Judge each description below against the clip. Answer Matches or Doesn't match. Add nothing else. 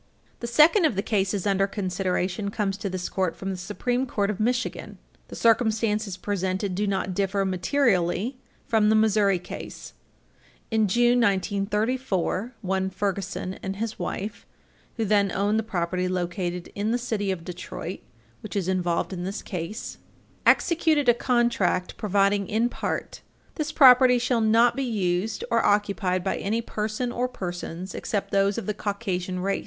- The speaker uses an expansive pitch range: Doesn't match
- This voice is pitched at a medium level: Doesn't match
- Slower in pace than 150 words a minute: Doesn't match